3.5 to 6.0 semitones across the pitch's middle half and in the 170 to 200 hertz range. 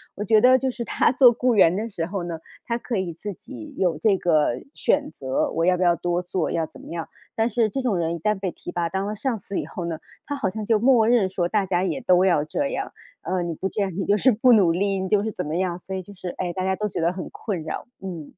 Yes: average, 4.0 semitones; high, 190 Hz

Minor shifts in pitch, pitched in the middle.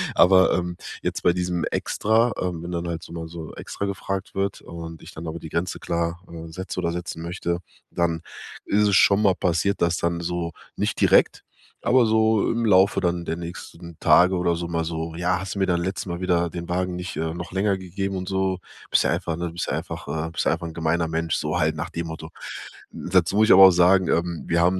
No: narrow, 2.0 semitones; very low, 85 Hz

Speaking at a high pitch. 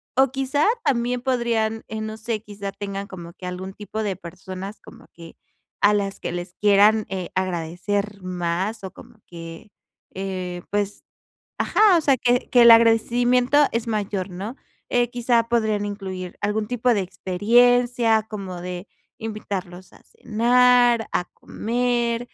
Yes: high, 210 Hz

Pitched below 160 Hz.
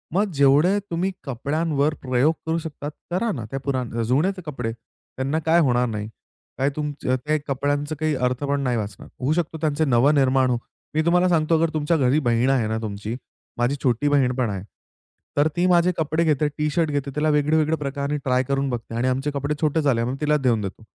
Yes: medium, 140 Hz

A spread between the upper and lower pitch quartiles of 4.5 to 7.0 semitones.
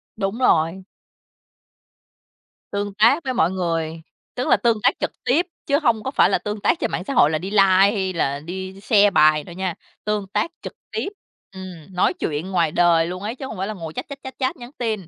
Yes: average, 4.8 semitones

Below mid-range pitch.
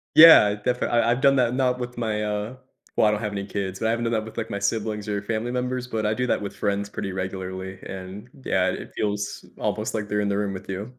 Yes: low, 105 Hz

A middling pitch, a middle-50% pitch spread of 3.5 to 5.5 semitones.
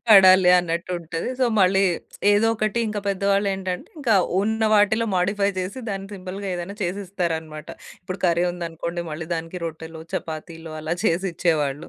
No: medium, 180 Hz; average, 3.1 semitones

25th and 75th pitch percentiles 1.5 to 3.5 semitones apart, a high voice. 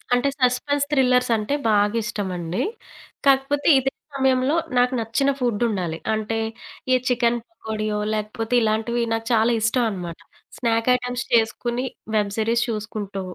Yes: average, 2.8 semitones; high, 230 Hz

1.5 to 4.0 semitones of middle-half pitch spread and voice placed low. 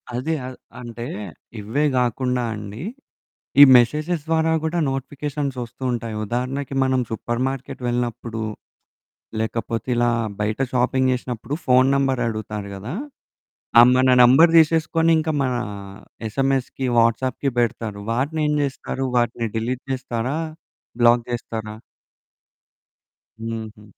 Yes: average, 2.8 semitones; low, 125 Hz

